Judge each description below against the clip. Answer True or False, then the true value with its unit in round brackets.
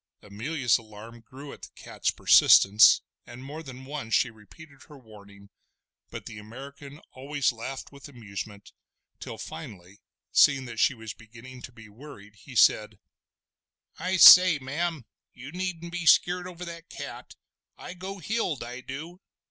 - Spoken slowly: False (150 wpm)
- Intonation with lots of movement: True (6.0 semitones)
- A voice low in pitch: True (130 Hz)